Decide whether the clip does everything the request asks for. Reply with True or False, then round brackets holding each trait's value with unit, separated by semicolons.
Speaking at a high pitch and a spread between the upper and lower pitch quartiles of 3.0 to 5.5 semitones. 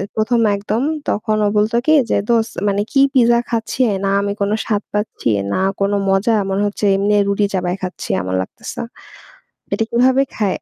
False (210 Hz; 2.6 semitones)